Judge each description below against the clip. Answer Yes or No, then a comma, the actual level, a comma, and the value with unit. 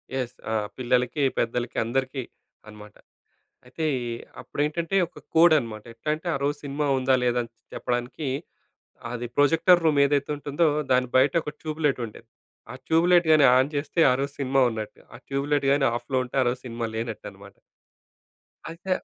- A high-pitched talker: No, low, 135 Hz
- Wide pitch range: No, average, 3.6 semitones